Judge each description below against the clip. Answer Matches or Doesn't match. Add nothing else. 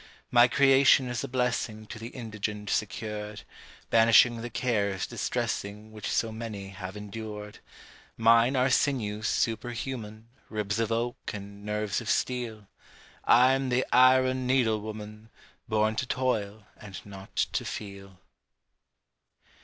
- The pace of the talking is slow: Matches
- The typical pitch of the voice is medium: Doesn't match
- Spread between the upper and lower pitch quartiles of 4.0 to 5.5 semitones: Doesn't match